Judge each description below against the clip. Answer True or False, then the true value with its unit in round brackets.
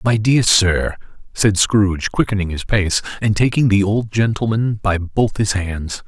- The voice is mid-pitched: False (100 Hz)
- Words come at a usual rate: True (170 wpm)